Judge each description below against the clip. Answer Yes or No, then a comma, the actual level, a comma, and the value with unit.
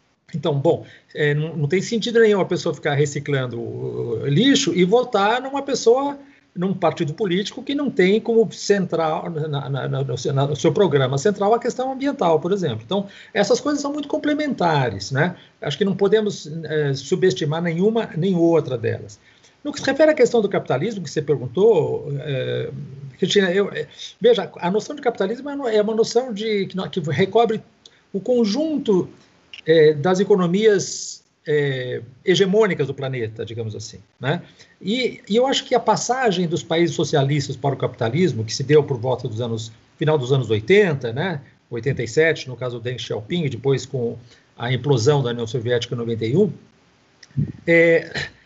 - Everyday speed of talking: Yes, average, 160 wpm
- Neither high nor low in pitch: Yes, medium, 165 Hz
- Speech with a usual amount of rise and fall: No, wide, 7.4 semitones